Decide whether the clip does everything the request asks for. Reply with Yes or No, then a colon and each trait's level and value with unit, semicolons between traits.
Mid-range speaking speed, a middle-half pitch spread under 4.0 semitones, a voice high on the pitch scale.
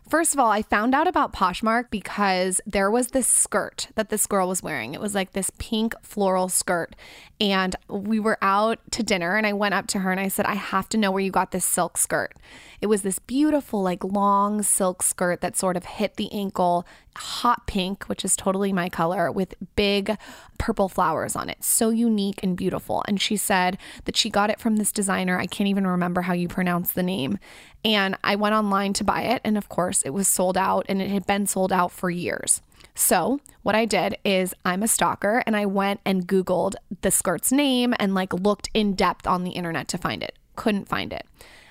No: fast, 220 wpm; narrow, 2.6 semitones; high, 200 Hz